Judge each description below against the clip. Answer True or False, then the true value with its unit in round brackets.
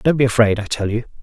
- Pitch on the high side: False (115 Hz)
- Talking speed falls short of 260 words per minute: False (295 wpm)